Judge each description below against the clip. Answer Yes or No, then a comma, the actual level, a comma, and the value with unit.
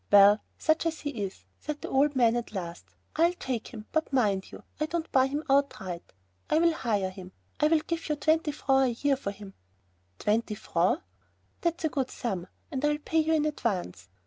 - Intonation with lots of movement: Yes, wide, 6.9 semitones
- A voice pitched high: Yes, very high, 265 Hz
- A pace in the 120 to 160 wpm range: No, average, 190 wpm